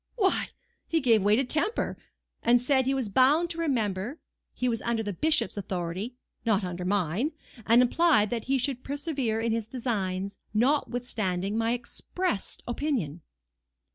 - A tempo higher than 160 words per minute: No, average, 150 wpm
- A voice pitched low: No, high, 235 Hz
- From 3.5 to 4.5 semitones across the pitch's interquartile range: No, average, 5.0 semitones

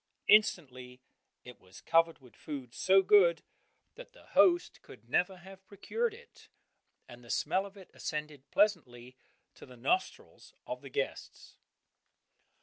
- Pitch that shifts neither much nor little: No, wide, 7.9 semitones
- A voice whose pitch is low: No, medium, 170 Hz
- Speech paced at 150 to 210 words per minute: No, average, 140 wpm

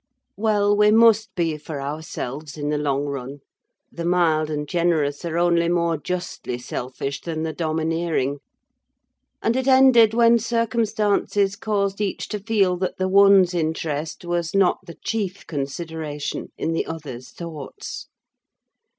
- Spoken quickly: No, average, 140 wpm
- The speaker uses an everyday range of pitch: Yes, average, 5.0 semitones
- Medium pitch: Yes, medium, 170 Hz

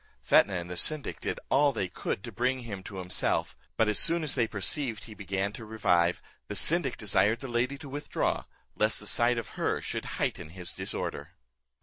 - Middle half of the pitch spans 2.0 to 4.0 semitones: No, average, 4.8 semitones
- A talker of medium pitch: No, low, 110 Hz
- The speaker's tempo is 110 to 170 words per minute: No, average, 200 wpm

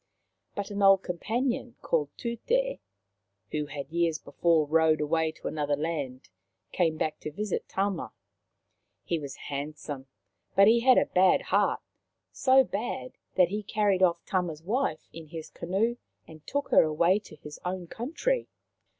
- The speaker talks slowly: No, average, 155 wpm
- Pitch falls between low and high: Yes, medium, 170 Hz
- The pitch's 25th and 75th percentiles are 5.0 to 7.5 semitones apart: Yes, wide, 5.4 semitones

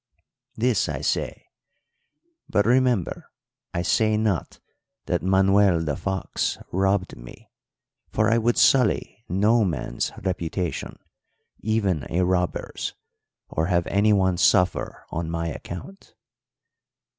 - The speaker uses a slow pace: Yes, slow, 110 wpm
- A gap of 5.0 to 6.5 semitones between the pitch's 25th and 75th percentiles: No, average, 3.7 semitones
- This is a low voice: Yes, very low, 95 Hz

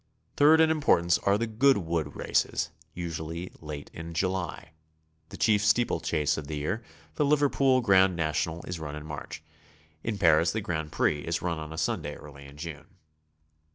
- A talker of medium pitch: No, very low, 85 Hz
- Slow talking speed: No, average, 165 wpm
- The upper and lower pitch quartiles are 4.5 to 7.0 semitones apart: Yes, average, 5.3 semitones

